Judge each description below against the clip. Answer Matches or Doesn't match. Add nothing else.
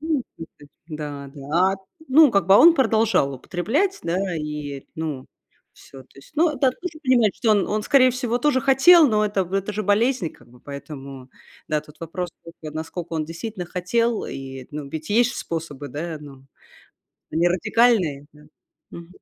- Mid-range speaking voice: Matches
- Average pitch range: Doesn't match